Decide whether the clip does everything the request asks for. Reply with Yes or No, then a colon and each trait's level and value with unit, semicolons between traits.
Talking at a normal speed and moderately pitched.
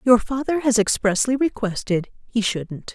No: average, 145 wpm; high, 225 Hz